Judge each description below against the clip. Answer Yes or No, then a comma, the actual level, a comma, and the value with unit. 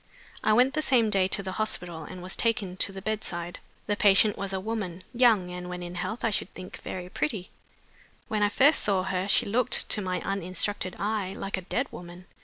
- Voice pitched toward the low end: No, high, 195 Hz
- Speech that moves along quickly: Yes, fast, 210 wpm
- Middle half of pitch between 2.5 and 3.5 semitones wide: Yes, average, 2.9 semitones